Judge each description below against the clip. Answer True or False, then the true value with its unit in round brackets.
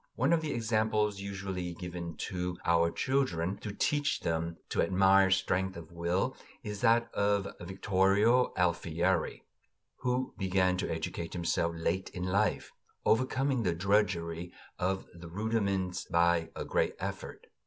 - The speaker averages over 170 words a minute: False (135 wpm)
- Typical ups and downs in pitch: True (3.6 semitones)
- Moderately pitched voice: False (95 Hz)